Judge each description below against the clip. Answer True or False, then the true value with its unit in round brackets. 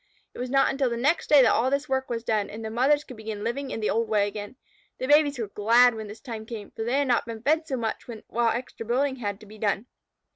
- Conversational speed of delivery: False (270 wpm)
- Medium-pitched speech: False (235 Hz)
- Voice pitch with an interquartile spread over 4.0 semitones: False (3.4 semitones)